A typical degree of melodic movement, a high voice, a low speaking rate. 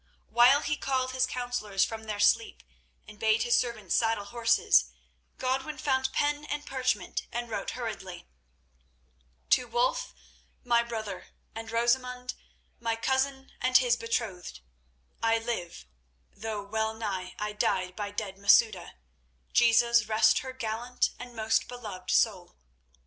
Yes: average, 3.5 semitones; high, 230 Hz; slow, 125 wpm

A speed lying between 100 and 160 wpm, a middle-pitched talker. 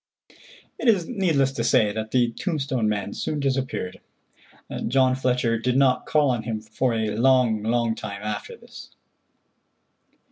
No: average, 145 wpm; low, 125 Hz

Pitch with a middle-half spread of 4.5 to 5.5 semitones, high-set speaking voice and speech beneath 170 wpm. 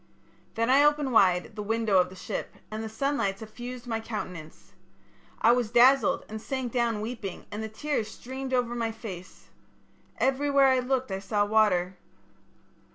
No: average, 3.7 semitones; high, 225 Hz; average, 160 wpm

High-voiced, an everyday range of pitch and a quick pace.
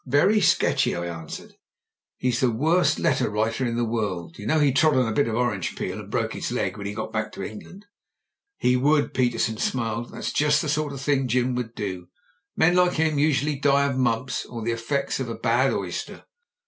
No: low, 125 Hz; average, 4.3 semitones; fast, 215 wpm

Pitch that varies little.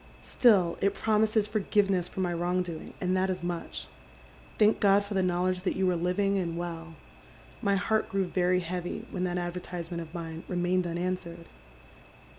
Yes: narrow, 2.1 semitones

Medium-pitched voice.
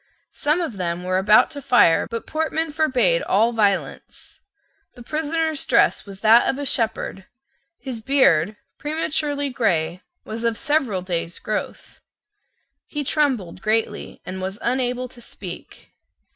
No: high, 235 Hz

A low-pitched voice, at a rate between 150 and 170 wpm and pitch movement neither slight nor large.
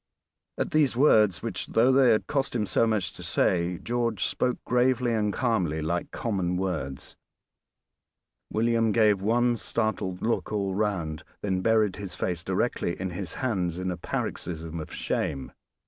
Yes: low, 105 Hz; average, 155 wpm; average, 4.6 semitones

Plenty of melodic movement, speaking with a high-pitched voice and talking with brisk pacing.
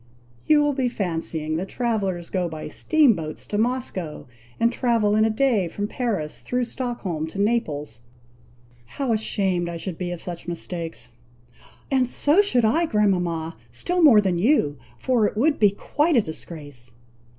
No: wide, 6.7 semitones; high, 205 Hz; average, 160 wpm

